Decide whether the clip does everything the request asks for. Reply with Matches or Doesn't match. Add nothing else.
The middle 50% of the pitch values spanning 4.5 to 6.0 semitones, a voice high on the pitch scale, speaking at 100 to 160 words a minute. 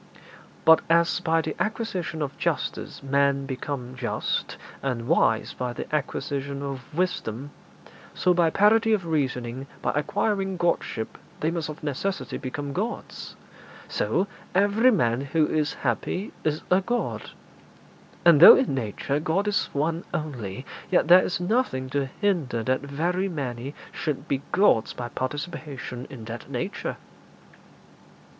Doesn't match